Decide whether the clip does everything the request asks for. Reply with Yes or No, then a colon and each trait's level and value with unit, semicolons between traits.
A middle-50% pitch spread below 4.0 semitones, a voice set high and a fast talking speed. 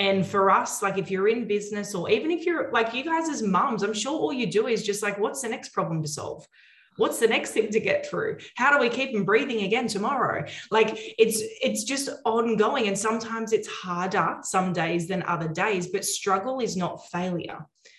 Yes: average, 3.3 semitones; high, 215 Hz; fast, 215 wpm